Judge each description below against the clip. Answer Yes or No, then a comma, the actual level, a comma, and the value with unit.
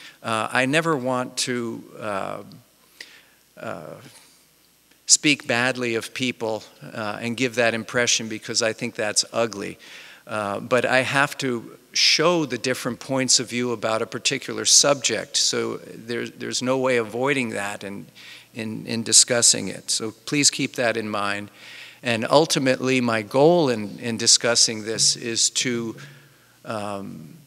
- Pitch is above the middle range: No, low, 120 Hz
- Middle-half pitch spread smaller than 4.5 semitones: Yes, narrow, 2.6 semitones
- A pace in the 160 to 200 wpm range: No, average, 140 wpm